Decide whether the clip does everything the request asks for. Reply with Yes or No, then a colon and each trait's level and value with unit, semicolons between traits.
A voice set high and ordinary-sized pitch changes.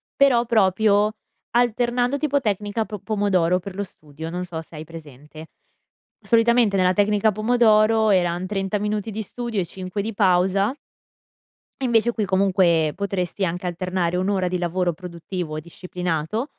Yes: high, 195 Hz; average, 3.5 semitones